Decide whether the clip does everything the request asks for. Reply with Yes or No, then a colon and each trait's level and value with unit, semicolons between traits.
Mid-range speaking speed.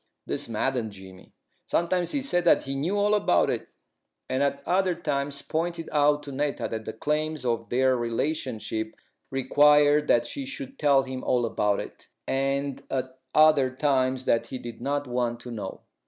Yes: average, 170 wpm